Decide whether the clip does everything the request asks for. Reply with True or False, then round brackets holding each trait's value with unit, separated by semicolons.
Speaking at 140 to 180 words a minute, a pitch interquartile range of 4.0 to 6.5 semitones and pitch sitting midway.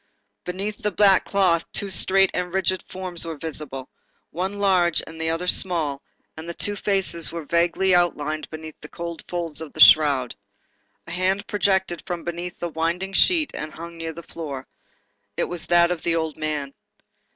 False (175 wpm; 2.7 semitones; 170 Hz)